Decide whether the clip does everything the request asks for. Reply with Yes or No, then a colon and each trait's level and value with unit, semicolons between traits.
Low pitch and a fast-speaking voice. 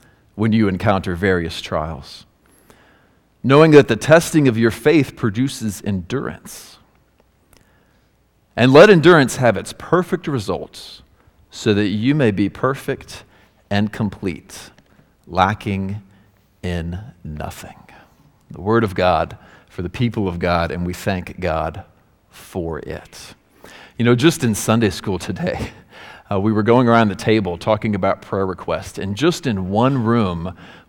No: low, 105 Hz; slow, 135 wpm